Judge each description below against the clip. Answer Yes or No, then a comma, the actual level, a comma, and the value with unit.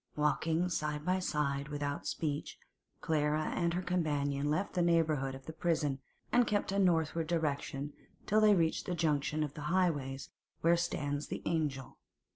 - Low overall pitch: No, medium, 155 Hz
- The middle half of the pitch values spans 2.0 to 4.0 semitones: Yes, average, 3.0 semitones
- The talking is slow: No, average, 155 wpm